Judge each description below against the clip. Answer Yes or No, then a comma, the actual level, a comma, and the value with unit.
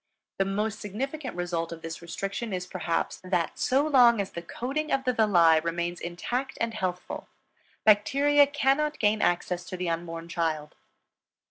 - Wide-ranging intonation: Yes, wide, 6.7 semitones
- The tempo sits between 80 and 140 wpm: No, average, 155 wpm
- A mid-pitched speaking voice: No, high, 195 Hz